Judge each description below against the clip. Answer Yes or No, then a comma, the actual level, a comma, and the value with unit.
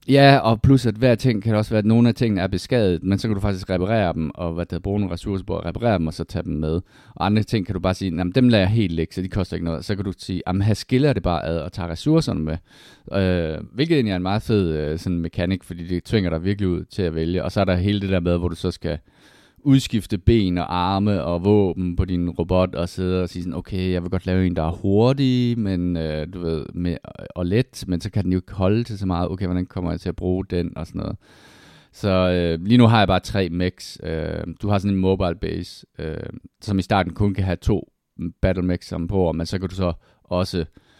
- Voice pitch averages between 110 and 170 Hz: No, very low, 95 Hz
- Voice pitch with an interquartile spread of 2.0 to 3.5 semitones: Yes, average, 2.9 semitones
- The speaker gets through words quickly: Yes, fast, 265 wpm